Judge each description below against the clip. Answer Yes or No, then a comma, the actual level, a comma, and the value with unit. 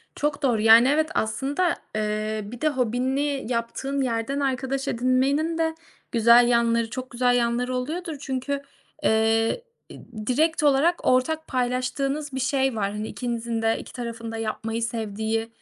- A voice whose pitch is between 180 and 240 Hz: No, very high, 250 Hz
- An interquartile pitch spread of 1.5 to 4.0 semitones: Yes, average, 3.4 semitones